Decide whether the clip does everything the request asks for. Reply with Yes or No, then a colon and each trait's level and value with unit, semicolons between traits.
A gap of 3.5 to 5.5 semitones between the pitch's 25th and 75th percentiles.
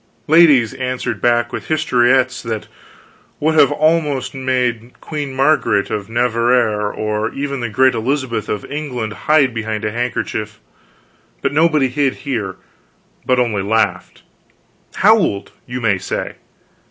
Yes: average, 4.2 semitones